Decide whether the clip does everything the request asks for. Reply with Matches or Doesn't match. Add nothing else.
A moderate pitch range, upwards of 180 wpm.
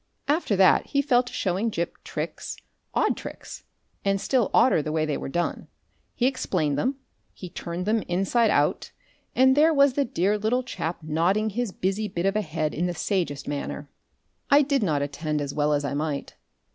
Doesn't match